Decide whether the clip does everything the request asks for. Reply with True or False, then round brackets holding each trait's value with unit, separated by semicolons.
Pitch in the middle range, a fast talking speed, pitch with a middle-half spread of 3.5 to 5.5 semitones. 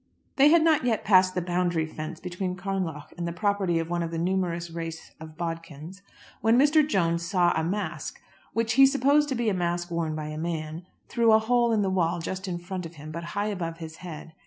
True (175 Hz; 225 wpm; 3.8 semitones)